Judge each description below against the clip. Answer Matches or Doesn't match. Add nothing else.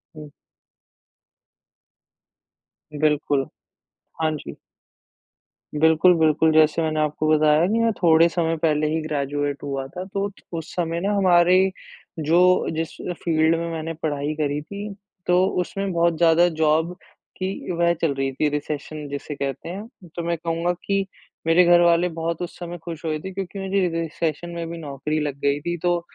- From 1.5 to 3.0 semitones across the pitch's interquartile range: Matches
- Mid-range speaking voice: Matches